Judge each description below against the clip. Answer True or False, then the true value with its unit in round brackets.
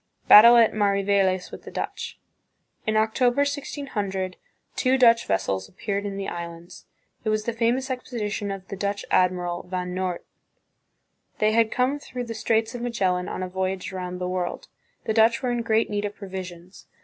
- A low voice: False (205 Hz)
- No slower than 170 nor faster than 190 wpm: True (180 wpm)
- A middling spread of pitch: True (3.9 semitones)